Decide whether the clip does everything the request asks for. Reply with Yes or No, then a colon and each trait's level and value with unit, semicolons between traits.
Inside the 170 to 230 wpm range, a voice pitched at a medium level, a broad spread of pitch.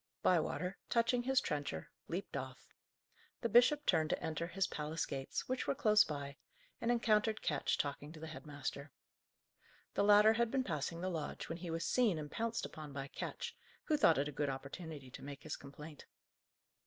Yes: average, 185 wpm; medium, 165 Hz; wide, 7.1 semitones